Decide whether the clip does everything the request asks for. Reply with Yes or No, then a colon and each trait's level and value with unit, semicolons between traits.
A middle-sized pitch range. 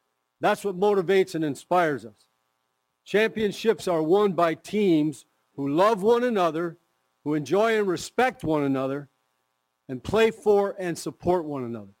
No: wide, 8.2 semitones